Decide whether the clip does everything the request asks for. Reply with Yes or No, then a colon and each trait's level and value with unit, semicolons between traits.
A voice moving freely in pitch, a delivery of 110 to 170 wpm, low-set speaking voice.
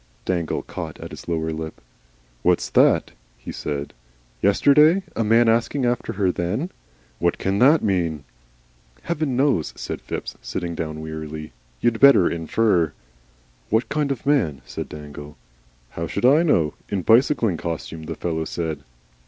Yes: wide, 7.5 semitones; average, 145 wpm; very low, 90 Hz